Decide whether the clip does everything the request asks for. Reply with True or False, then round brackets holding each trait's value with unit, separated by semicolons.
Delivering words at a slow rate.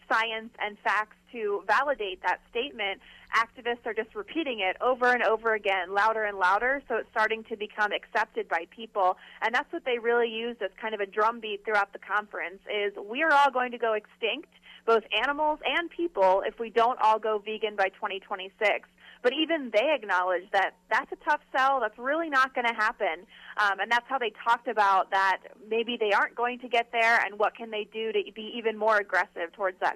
False (205 wpm)